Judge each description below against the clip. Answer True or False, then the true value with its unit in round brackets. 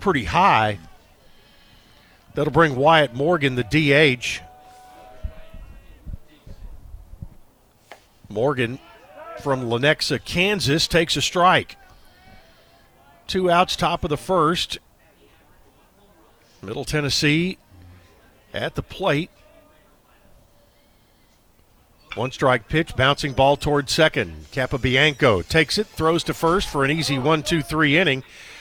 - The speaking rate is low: True (95 wpm)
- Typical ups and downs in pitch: False (6.9 semitones)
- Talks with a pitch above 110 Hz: True (140 Hz)